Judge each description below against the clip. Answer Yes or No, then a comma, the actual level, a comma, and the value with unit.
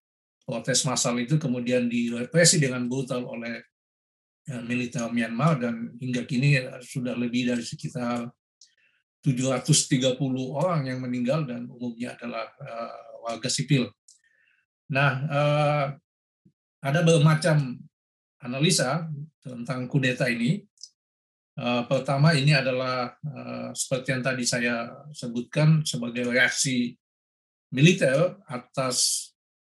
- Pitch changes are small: No, average, 3.2 semitones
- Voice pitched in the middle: No, low, 130 Hz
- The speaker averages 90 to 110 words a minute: Yes, average, 100 wpm